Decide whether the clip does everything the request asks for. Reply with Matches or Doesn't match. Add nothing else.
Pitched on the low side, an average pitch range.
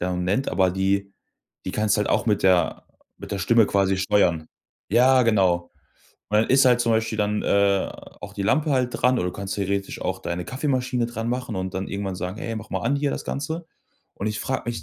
Matches